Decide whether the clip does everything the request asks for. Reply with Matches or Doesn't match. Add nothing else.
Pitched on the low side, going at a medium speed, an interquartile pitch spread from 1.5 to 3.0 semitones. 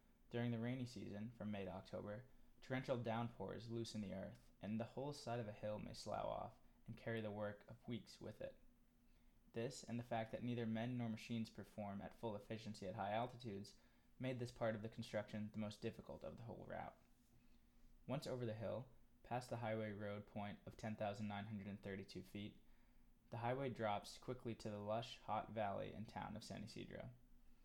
Matches